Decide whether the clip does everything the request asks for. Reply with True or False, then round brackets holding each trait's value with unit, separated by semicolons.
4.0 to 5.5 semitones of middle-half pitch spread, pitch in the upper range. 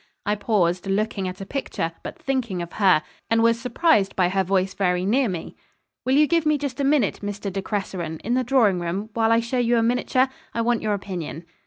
True (4.5 semitones; 210 Hz)